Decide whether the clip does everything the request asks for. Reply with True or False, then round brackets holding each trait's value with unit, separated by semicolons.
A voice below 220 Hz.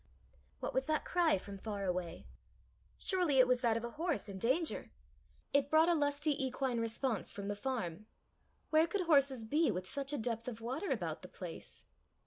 False (260 Hz)